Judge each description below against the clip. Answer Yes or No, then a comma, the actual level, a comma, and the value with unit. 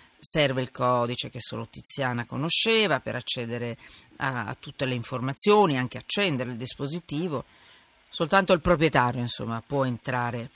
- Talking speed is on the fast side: No, average, 135 wpm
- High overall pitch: No, low, 130 Hz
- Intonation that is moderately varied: Yes, average, 4.9 semitones